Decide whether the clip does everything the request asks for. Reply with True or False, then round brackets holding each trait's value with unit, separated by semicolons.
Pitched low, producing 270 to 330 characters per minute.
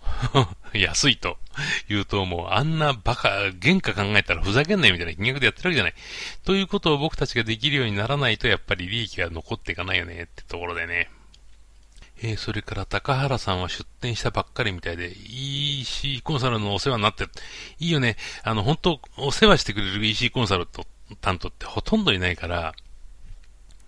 False (110 Hz; 400 characters per minute)